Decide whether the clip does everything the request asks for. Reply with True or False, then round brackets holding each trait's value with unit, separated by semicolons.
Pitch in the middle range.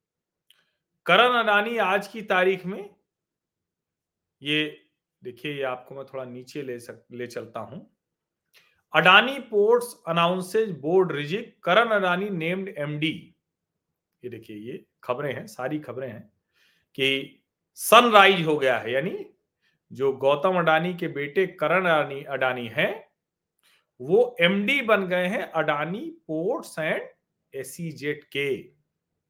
True (165 Hz)